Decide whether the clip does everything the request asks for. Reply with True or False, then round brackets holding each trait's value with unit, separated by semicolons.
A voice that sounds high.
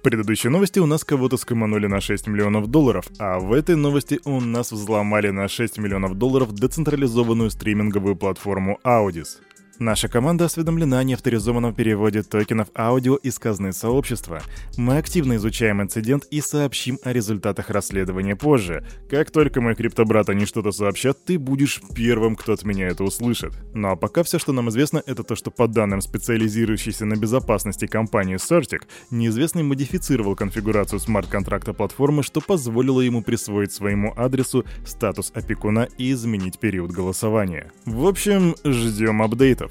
False (115 Hz)